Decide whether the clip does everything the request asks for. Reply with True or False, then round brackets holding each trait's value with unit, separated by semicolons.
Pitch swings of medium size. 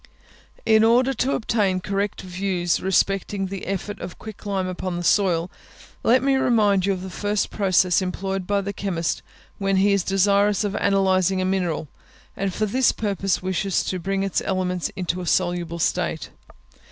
False (1.8 semitones)